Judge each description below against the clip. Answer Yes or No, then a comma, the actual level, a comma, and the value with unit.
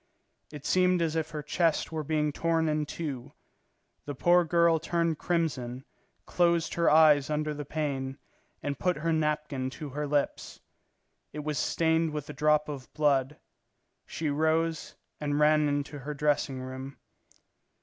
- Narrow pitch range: Yes, narrow, 2.0 semitones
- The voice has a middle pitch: Yes, medium, 150 Hz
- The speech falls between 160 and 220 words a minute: No, average, 150 wpm